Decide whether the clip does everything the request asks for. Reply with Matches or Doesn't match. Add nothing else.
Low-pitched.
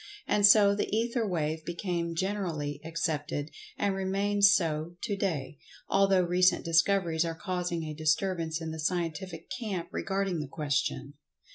Doesn't match